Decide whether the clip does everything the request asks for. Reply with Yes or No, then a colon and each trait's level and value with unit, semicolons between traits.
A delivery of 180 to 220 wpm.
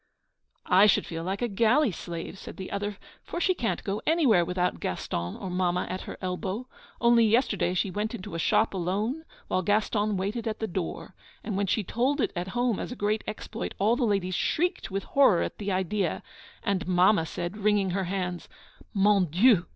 Yes: average, 195 wpm